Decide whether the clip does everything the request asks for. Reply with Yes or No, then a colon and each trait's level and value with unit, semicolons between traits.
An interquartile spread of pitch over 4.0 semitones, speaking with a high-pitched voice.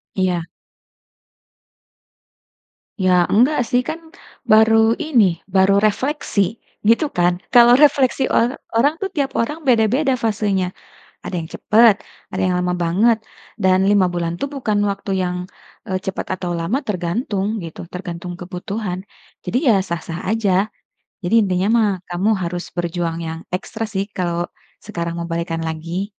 Yes: average, 4.4 semitones; high, 195 Hz